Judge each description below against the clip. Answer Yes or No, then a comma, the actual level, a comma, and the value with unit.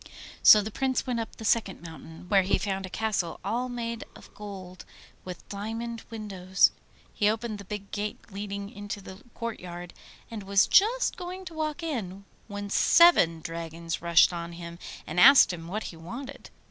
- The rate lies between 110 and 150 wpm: No, average, 170 wpm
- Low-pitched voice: No, high, 205 Hz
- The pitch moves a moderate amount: Yes, average, 4.4 semitones